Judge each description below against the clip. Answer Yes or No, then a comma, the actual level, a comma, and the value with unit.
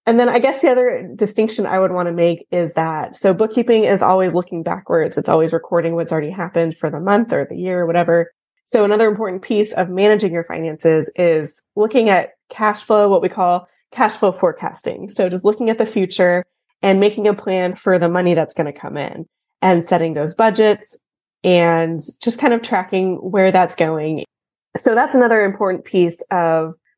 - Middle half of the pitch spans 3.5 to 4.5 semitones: Yes, average, 4.0 semitones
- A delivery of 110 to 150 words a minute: No, average, 200 wpm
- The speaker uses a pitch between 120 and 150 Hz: No, medium, 185 Hz